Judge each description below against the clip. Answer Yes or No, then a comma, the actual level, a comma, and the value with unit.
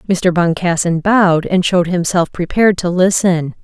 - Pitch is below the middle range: No, medium, 180 Hz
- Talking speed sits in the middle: Yes, average, 150 wpm